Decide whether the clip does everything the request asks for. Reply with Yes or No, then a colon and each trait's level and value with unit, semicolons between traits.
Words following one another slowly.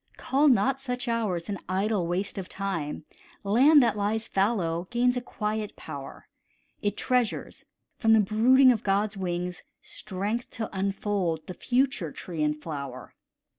No: average, 145 wpm